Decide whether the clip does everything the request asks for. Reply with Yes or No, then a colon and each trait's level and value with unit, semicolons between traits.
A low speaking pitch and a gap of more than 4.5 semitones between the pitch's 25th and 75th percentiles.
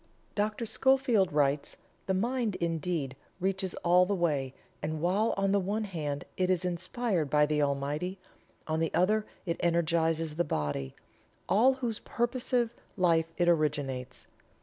No: medium, 175 Hz; average, 5.2 semitones